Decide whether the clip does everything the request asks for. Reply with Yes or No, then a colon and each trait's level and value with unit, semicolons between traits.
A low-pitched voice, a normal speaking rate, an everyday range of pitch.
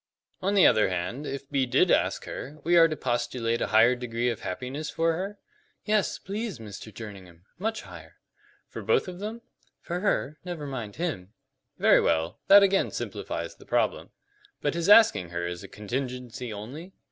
No: low, 130 Hz; average, 175 wpm; wide, 8.3 semitones